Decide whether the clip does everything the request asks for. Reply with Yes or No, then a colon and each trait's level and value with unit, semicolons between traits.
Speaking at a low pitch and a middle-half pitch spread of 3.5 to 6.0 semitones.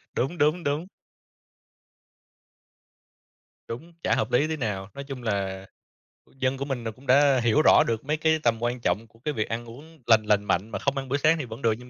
Yes: low, 125 Hz; average, 4.5 semitones